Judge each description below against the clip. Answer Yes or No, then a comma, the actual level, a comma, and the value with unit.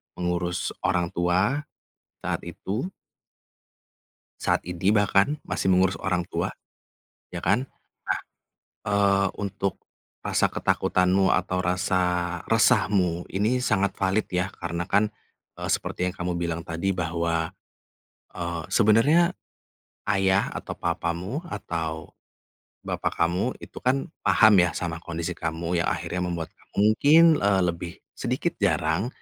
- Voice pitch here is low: Yes, very low, 90 Hz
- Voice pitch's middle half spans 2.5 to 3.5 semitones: Yes, average, 2.9 semitones